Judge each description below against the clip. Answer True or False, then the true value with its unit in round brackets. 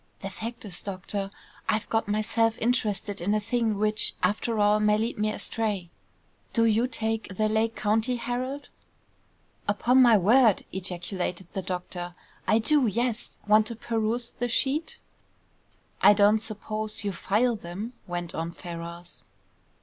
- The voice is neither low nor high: False (215 Hz)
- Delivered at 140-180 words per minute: True (145 wpm)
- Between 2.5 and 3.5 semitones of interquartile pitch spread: True (2.8 semitones)